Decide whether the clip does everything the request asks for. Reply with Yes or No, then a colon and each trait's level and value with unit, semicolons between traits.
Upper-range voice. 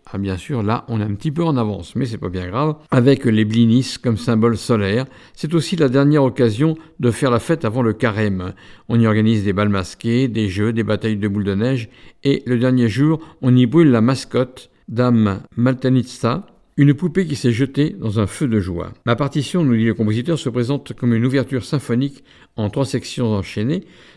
No: low, 120 Hz